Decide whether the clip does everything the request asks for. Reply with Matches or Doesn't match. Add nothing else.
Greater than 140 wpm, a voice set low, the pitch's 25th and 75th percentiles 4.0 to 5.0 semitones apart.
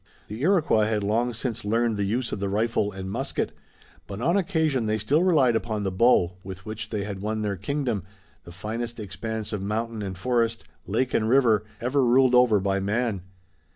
Doesn't match